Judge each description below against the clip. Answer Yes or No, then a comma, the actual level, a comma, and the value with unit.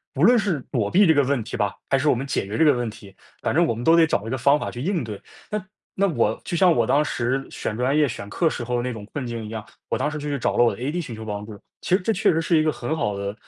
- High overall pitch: No, low, 130 Hz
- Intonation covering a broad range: Yes, wide, 5.9 semitones